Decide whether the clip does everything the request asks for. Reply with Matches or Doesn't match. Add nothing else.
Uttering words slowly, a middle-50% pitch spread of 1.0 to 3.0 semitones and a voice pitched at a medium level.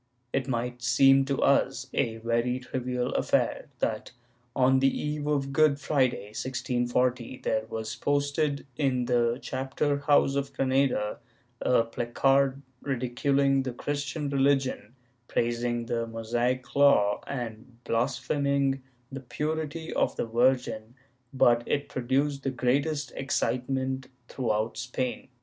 Doesn't match